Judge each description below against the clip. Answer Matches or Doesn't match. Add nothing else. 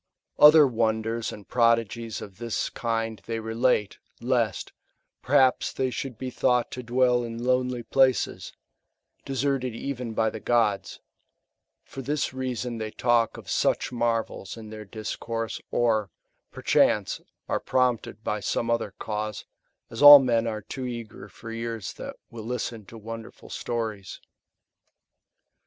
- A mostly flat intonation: Matches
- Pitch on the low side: Matches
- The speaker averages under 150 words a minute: Matches